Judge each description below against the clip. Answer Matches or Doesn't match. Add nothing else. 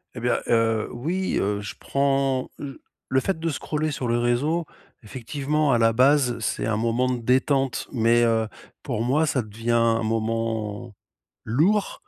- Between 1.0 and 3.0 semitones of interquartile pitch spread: Doesn't match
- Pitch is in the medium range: Doesn't match